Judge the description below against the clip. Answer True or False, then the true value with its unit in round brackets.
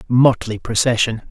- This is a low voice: True (115 Hz)